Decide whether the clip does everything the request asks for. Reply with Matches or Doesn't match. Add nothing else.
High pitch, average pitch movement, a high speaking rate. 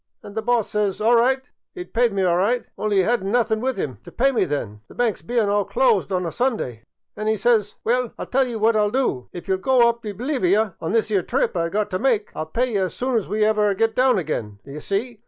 Matches